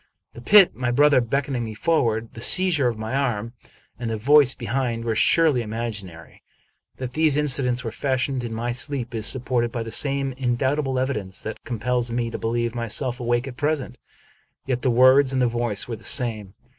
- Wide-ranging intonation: No, average, 2.8 semitones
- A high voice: No, low, 125 Hz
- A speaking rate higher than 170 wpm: Yes, average, 190 wpm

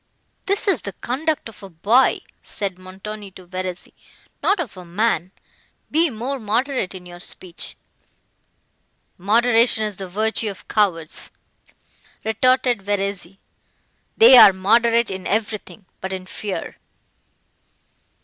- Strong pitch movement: No, average, 4.0 semitones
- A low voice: No, high, 210 Hz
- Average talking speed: No, slow, 120 wpm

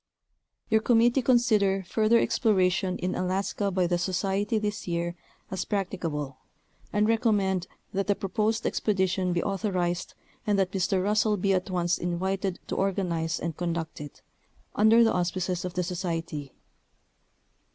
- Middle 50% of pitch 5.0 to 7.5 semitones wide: No, average, 2.8 semitones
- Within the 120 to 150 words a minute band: Yes, average, 140 wpm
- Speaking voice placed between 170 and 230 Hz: Yes, high, 190 Hz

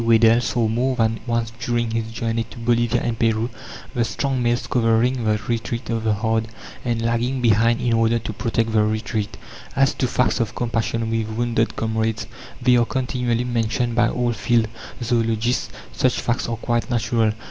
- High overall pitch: No, low, 115 Hz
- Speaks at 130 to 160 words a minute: No, average, 175 wpm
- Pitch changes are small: Yes, narrow, 1.2 semitones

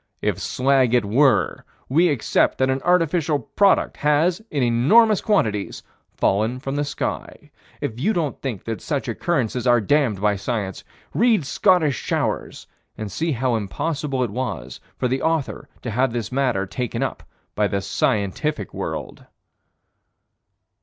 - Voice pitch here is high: No, low, 130 Hz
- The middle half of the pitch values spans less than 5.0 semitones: No, average, 5.3 semitones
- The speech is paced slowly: No, average, 145 wpm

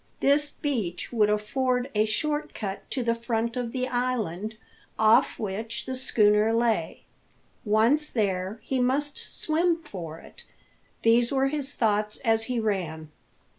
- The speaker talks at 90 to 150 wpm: Yes, average, 140 wpm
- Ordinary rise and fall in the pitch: Yes, average, 3.6 semitones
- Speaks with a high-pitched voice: Yes, high, 230 Hz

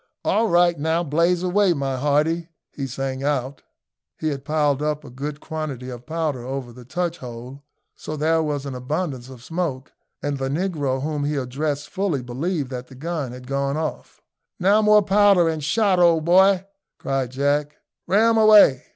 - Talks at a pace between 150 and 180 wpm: Yes, average, 175 wpm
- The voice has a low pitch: No, medium, 150 Hz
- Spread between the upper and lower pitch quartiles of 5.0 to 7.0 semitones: No, average, 4.3 semitones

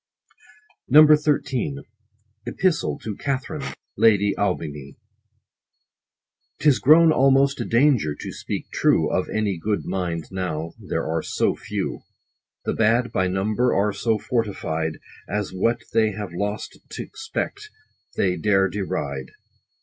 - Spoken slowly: Yes, slow, 125 wpm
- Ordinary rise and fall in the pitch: No, wide, 5.9 semitones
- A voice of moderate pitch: No, low, 105 Hz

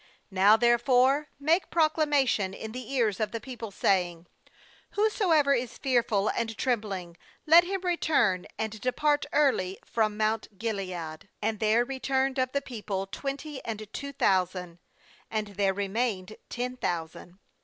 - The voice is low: No, high, 225 Hz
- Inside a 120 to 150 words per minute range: Yes, average, 140 wpm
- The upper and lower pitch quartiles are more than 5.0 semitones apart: Yes, wide, 5.6 semitones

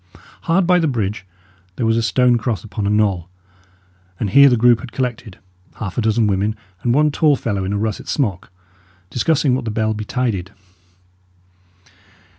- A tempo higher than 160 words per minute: Yes, average, 170 wpm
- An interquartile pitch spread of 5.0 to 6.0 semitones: No, average, 3.5 semitones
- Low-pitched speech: Yes, low, 115 Hz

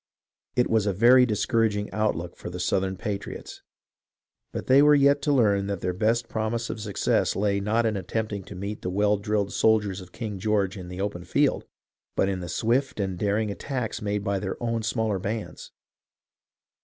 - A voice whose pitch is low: Yes, low, 105 Hz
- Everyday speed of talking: Yes, average, 190 wpm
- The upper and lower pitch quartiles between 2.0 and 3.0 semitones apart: Yes, narrow, 2.5 semitones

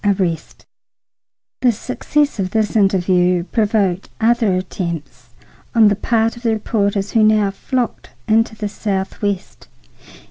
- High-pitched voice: Yes, high, 205 Hz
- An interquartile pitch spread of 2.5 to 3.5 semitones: Yes, average, 3.1 semitones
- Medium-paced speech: No, slow, 120 wpm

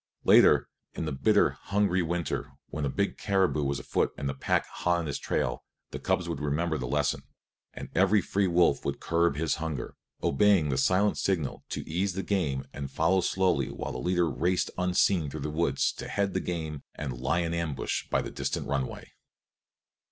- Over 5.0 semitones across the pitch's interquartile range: No, average, 4.3 semitones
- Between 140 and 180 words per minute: No, average, 190 wpm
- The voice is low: Yes, very low, 85 Hz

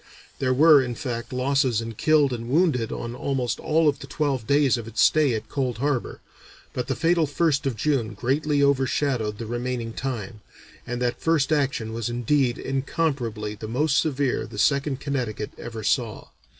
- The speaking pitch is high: No, low, 130 Hz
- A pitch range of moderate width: Yes, average, 3.5 semitones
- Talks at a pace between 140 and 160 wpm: No, average, 175 wpm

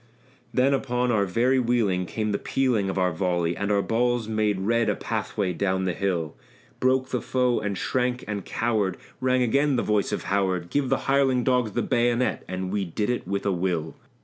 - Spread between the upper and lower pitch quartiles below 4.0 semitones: No, average, 4.7 semitones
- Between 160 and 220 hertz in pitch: No, low, 110 Hz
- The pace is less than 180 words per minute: No, average, 200 wpm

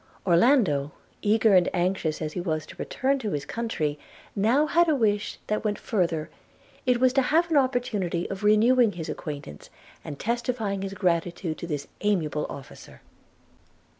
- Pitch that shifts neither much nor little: No, wide, 6.3 semitones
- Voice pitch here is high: Yes, high, 200 Hz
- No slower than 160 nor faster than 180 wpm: Yes, average, 165 wpm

